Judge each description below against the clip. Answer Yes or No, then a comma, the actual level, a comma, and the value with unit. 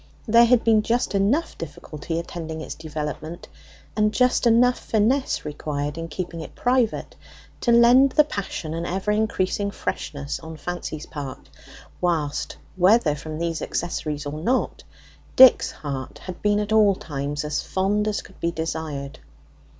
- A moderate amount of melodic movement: No, wide, 6.0 semitones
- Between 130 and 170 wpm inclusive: Yes, average, 150 wpm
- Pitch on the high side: No, medium, 175 Hz